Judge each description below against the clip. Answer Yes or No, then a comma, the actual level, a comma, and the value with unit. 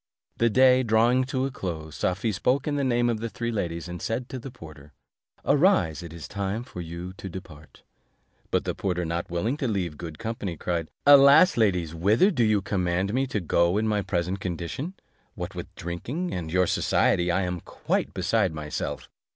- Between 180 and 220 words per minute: Yes, average, 190 wpm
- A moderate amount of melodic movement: No, wide, 5.8 semitones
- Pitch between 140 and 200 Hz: No, low, 100 Hz